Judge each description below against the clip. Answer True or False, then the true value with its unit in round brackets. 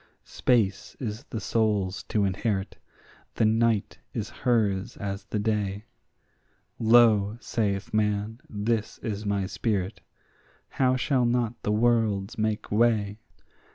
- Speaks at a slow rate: True (120 wpm)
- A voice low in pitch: True (105 Hz)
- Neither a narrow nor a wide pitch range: False (2.3 semitones)